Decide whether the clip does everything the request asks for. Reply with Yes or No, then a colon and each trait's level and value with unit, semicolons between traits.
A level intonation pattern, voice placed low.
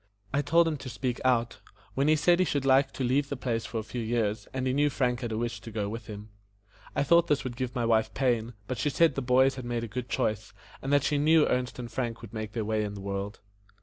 No: average, 3.5 semitones; low, 125 Hz